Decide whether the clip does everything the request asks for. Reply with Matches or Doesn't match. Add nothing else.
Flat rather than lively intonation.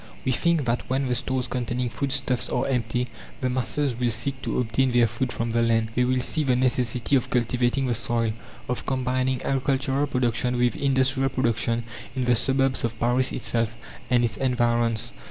Matches